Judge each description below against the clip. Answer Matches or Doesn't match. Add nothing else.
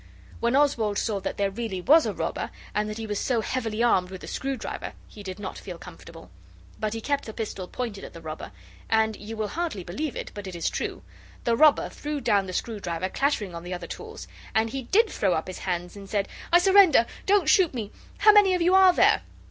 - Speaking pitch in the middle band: Doesn't match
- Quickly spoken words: Matches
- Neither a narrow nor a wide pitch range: Doesn't match